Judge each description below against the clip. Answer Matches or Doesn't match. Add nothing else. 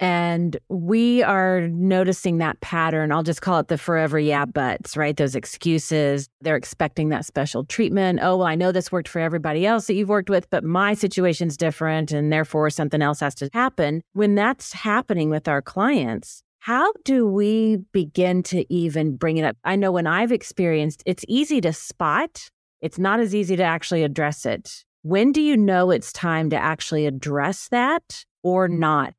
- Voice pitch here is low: Doesn't match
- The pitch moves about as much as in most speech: Matches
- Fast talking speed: Doesn't match